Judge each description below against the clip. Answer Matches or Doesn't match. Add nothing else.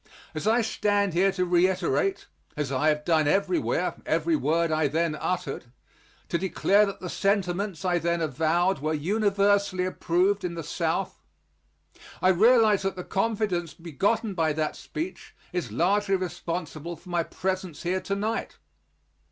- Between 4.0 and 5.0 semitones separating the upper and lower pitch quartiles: Doesn't match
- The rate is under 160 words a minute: Matches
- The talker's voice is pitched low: Doesn't match